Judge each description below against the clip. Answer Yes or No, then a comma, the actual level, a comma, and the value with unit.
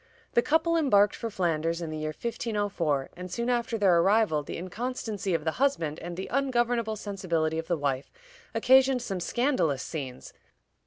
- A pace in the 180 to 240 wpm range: No, average, 165 wpm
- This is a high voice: Yes, high, 195 Hz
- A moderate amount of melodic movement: No, wide, 6.6 semitones